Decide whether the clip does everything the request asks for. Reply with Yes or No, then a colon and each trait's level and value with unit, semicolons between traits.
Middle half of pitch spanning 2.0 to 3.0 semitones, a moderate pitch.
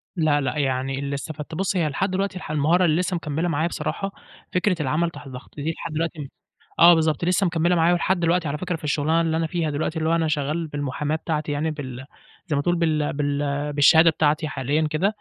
Yes: narrow, 2.6 semitones; medium, 155 Hz